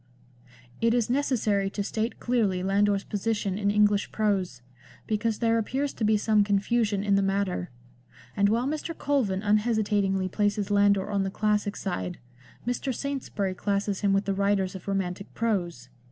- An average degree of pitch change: No, narrow, 2.3 semitones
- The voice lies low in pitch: No, high, 205 Hz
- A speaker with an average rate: Yes, average, 160 wpm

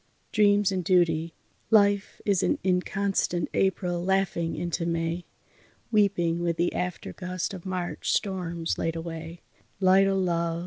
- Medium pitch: Yes, medium, 180 Hz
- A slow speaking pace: Yes, slow, 130 wpm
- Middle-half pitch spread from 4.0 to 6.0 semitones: No, narrow, 2.4 semitones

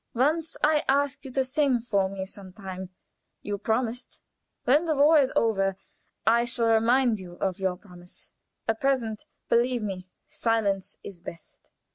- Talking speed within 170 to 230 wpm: No, average, 155 wpm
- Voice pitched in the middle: No, high, 225 Hz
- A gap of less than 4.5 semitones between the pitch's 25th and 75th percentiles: No, wide, 5.4 semitones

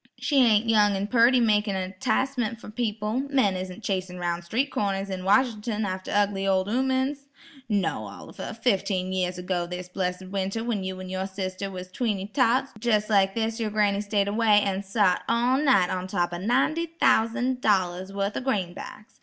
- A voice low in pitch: No, high, 205 Hz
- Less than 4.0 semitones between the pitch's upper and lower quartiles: Yes, average, 3.6 semitones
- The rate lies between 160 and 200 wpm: Yes, average, 180 wpm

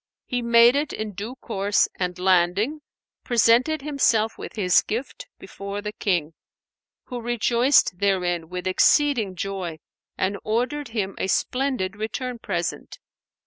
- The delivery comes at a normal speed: No, slow, 130 wpm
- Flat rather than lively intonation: No, average, 4.8 semitones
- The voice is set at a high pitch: Yes, high, 215 Hz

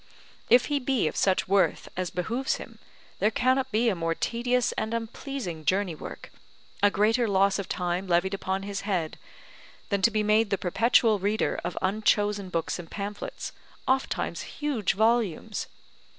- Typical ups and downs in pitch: Yes, average, 3.7 semitones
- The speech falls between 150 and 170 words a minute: Yes, average, 160 wpm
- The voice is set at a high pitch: Yes, high, 205 Hz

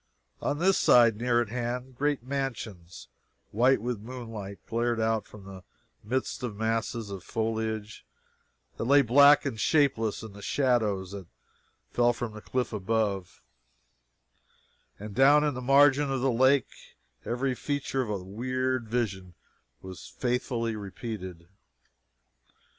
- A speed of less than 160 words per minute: Yes, slow, 135 wpm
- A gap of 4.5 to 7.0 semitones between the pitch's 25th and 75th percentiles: No, average, 3.6 semitones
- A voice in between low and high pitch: No, low, 115 Hz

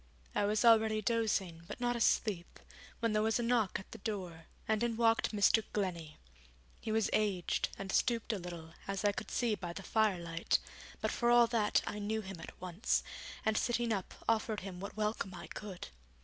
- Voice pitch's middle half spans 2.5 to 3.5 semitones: Yes, average, 3.2 semitones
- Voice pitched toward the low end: No, high, 210 Hz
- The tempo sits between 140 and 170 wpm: No, average, 190 wpm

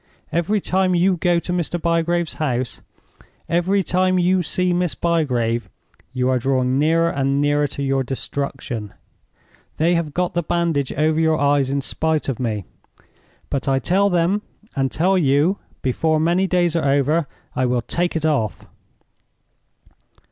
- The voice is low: No, medium, 160 Hz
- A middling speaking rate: Yes, average, 155 wpm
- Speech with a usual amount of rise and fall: Yes, average, 4.3 semitones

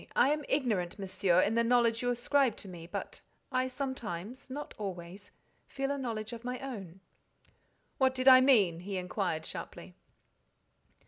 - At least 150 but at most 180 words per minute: Yes, average, 155 wpm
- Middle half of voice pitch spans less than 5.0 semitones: No, wide, 5.5 semitones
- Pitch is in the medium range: No, high, 230 Hz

